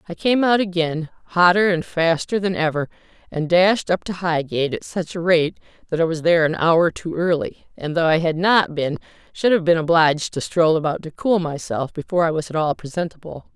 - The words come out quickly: Yes, fast, 210 wpm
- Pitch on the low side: No, medium, 170 Hz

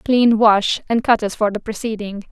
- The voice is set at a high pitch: Yes, high, 215 Hz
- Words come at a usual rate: No, fast, 210 wpm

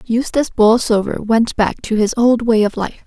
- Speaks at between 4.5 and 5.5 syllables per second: Yes, 4.8 syllables/s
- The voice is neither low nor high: No, high, 225 Hz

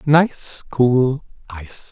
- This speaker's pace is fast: No, slow, 95 wpm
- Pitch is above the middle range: No, low, 135 Hz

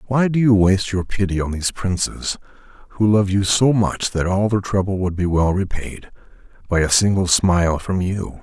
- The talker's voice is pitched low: Yes, very low, 95 Hz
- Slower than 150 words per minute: No, average, 200 wpm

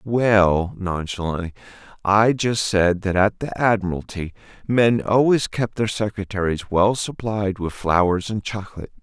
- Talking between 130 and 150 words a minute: Yes, slow, 135 wpm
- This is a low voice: Yes, low, 100 Hz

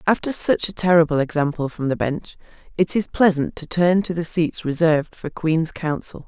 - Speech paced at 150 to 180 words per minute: No, average, 190 wpm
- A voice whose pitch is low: No, medium, 165 Hz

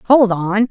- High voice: Yes, high, 210 Hz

